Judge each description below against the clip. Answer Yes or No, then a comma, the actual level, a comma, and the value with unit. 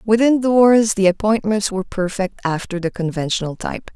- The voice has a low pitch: No, high, 205 Hz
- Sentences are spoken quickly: No, average, 150 wpm